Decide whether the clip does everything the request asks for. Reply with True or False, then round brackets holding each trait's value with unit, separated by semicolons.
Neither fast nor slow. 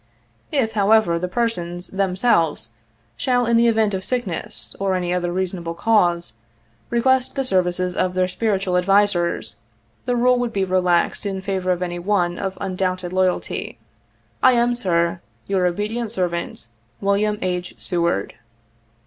True (150 wpm)